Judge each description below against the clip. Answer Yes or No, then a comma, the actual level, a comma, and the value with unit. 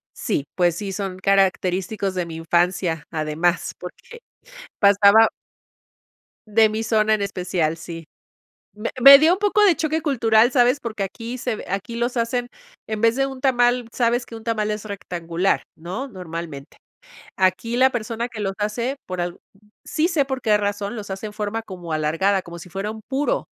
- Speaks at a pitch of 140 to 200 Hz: No, high, 210 Hz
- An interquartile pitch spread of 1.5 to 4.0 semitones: No, average, 4.7 semitones